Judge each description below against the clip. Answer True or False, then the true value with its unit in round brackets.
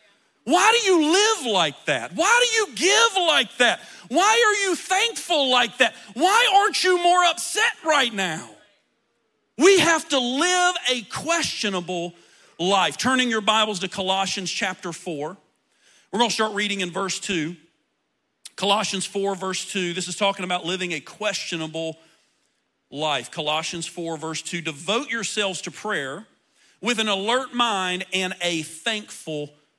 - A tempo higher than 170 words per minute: False (150 wpm)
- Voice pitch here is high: True (205 Hz)